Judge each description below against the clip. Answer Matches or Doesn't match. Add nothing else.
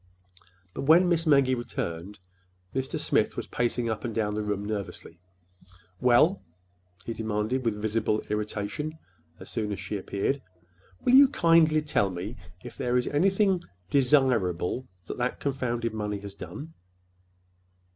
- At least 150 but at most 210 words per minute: Doesn't match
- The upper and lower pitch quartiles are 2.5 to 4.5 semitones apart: Doesn't match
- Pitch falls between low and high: Doesn't match